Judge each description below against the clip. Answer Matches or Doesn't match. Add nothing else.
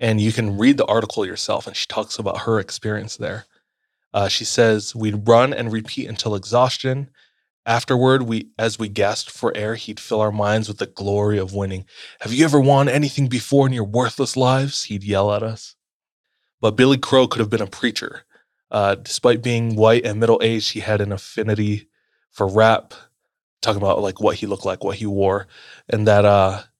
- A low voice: Matches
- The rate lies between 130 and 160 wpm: Doesn't match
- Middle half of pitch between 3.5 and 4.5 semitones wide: Doesn't match